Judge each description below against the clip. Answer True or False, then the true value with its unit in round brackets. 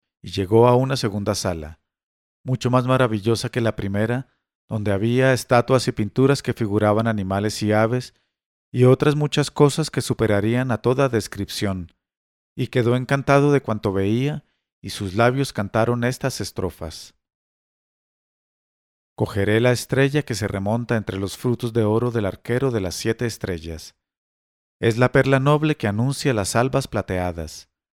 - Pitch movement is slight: False (4.0 semitones)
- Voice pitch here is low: True (115 Hz)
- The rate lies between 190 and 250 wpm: False (150 wpm)